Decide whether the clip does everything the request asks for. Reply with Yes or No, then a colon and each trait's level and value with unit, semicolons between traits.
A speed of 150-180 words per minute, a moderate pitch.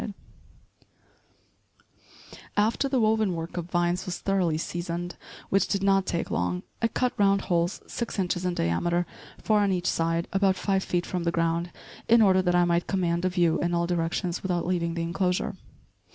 Yes: average, 175 wpm; medium, 175 Hz